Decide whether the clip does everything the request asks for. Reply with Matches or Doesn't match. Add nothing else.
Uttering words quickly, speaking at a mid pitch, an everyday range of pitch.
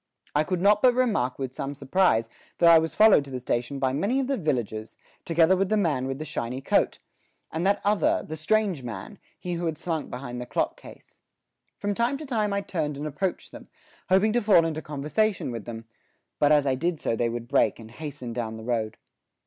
Doesn't match